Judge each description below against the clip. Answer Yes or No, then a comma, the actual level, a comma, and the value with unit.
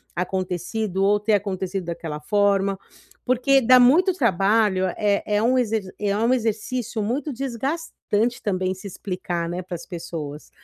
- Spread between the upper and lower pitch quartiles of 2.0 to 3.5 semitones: No, average, 4.2 semitones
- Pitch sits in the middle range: No, high, 205 Hz